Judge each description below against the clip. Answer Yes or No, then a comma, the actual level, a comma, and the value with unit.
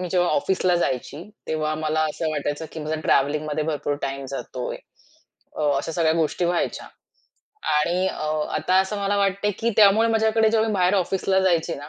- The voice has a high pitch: No, medium, 170 Hz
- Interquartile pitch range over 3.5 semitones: Yes, average, 4.3 semitones